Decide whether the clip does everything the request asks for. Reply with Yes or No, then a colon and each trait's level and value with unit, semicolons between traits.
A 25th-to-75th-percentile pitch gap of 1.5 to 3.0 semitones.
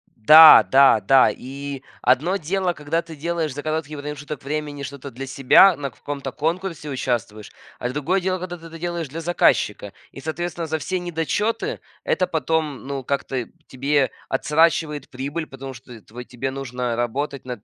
No: average, 3.7 semitones